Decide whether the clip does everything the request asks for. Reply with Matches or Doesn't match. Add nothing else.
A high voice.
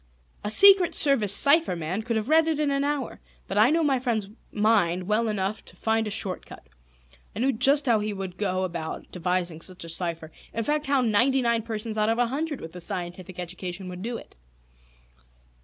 Matches